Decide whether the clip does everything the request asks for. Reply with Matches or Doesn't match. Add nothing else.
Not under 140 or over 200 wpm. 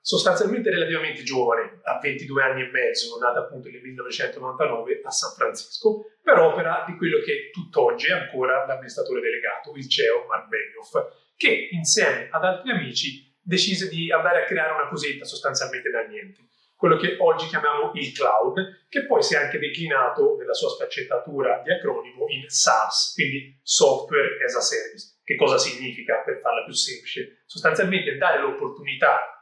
Matches